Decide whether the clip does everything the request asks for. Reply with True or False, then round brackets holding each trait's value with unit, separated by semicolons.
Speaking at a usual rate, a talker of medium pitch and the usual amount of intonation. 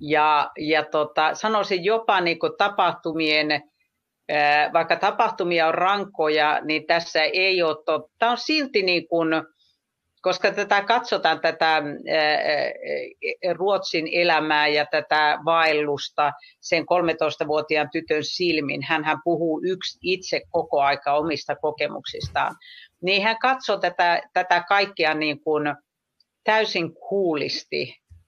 True (110 wpm; 165 Hz; 3.7 semitones)